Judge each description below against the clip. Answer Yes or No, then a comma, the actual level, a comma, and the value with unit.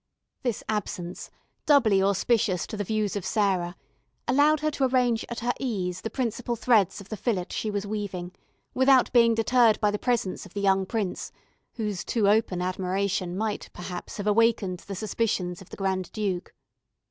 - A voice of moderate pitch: No, high, 210 Hz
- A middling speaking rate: Yes, average, 170 wpm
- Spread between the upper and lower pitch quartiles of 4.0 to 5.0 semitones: No, average, 3.6 semitones